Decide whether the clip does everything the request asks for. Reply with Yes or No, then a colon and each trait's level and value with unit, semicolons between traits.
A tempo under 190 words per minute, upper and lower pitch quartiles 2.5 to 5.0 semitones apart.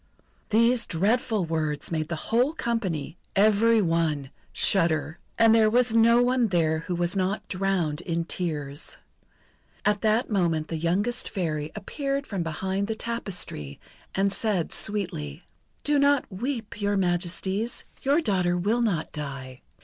No: average, 140 wpm; wide, 5.6 semitones